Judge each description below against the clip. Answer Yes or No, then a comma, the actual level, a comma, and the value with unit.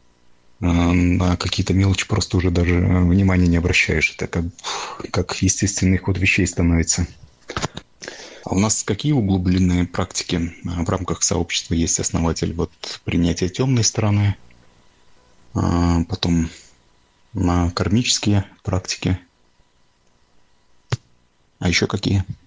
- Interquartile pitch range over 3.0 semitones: No, narrow, 2.4 semitones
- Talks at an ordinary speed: No, slow, 105 wpm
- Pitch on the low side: Yes, very low, 90 Hz